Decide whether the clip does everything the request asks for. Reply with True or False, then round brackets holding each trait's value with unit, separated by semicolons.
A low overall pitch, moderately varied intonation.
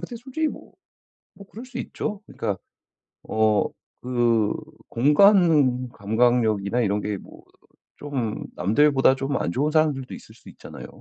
False (125 Hz; 5.9 semitones)